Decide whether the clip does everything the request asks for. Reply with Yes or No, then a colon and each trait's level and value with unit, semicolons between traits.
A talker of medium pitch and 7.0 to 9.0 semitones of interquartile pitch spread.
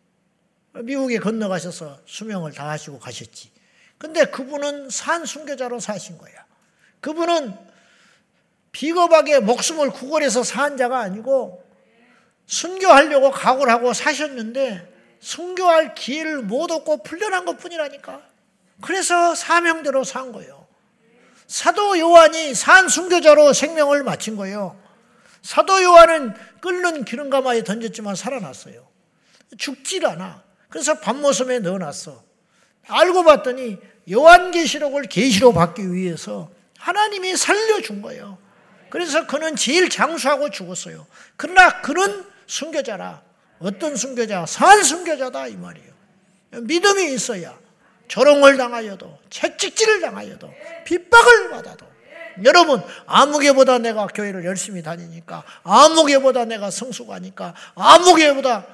No: very high, 265 Hz; wide, 7.7 semitones